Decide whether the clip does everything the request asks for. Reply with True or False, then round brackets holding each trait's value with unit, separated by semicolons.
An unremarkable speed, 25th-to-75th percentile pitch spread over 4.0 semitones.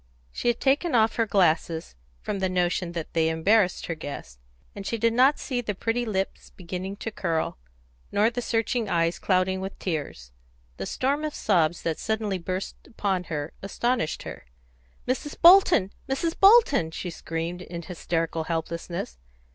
True (160 wpm; 5.6 semitones)